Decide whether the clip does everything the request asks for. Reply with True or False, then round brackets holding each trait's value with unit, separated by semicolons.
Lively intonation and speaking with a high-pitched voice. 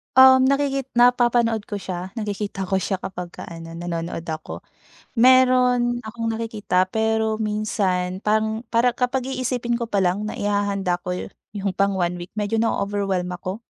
False (4.2 semitones; 210 Hz)